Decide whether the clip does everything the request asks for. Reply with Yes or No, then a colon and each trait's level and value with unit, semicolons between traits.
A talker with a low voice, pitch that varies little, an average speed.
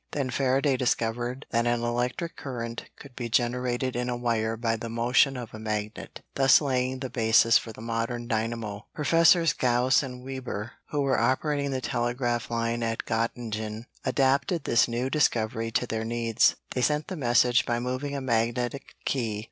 Yes: low, 120 Hz; narrow, 2.3 semitones; average, 170 wpm